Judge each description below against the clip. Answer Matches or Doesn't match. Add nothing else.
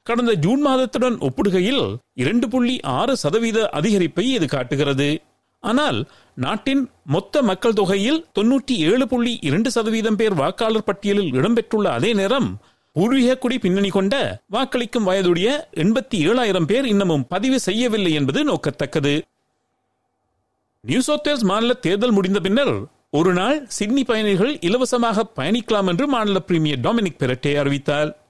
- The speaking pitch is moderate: Doesn't match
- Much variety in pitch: Matches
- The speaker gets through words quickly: Doesn't match